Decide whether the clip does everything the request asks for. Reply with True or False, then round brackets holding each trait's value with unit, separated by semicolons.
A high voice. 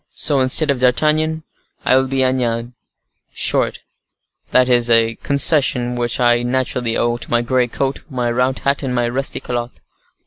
False (125 Hz)